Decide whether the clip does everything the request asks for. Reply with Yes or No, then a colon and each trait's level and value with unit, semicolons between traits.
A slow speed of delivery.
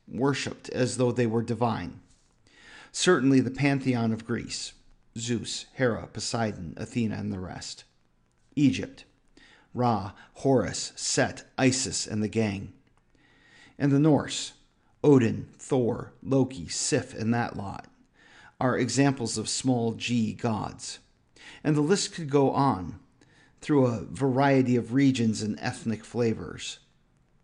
Yes: slow, 120 wpm